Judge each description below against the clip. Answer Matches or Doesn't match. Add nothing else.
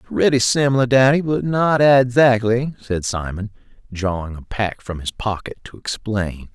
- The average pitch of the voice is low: Matches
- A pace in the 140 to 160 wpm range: Matches